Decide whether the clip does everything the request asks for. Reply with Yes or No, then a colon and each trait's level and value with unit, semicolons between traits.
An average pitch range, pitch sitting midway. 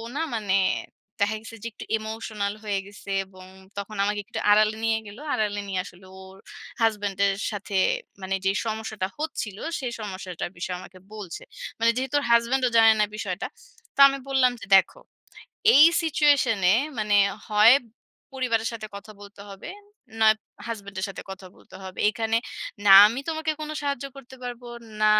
No: average, 3.0 semitones; high, 215 Hz